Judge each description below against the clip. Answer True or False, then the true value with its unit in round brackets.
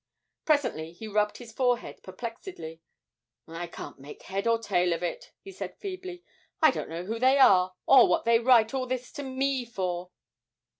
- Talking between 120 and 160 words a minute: False (180 wpm)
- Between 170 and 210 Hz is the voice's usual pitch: False (230 Hz)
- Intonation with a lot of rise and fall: True (6.5 semitones)